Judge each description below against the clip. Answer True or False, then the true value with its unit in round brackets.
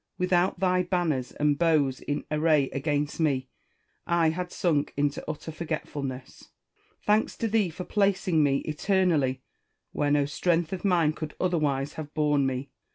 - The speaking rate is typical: True (150 wpm)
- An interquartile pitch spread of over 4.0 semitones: False (3.6 semitones)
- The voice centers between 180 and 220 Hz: False (155 Hz)